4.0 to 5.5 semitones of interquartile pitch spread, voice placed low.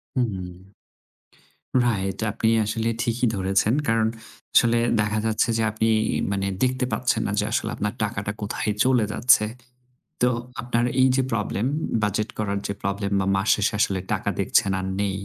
No: average, 2.8 semitones; low, 105 Hz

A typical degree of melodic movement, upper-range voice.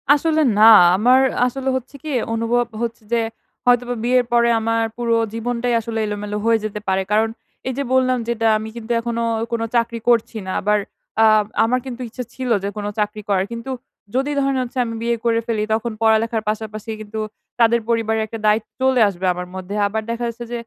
No: narrow, 1.9 semitones; high, 230 Hz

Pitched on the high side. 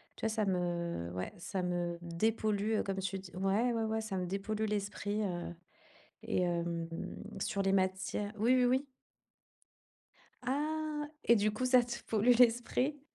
Yes: high, 205 Hz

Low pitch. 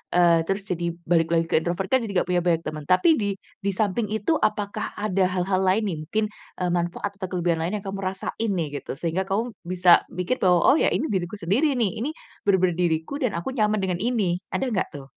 No: medium, 185 Hz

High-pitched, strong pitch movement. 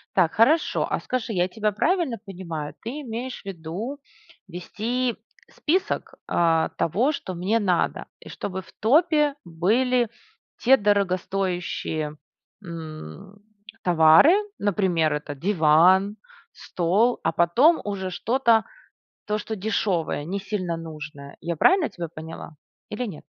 Yes: high, 195 Hz; wide, 5.7 semitones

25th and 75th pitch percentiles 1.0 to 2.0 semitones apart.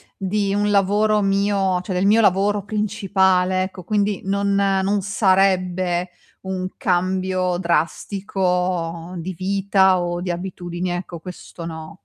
Yes: narrow, 1.7 semitones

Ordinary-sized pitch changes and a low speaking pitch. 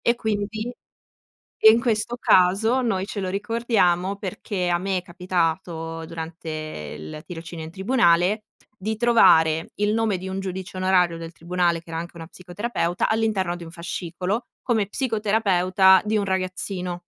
No: average, 3.6 semitones; medium, 185 Hz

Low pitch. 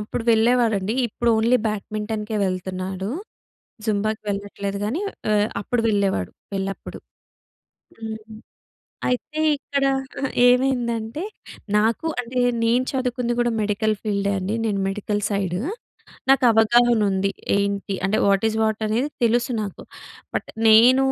No: high, 220 Hz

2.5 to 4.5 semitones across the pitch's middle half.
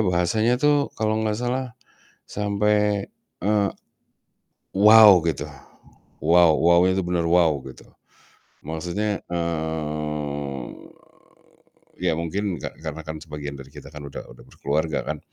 No: average, 5.2 semitones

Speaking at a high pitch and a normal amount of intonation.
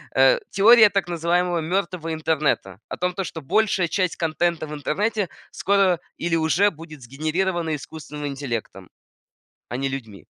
No: medium, 165 Hz; average, 3.8 semitones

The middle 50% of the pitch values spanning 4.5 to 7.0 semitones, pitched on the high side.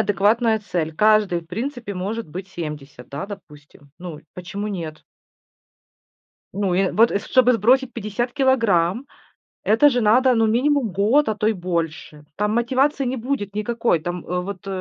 Yes: average, 5.0 semitones; high, 205 Hz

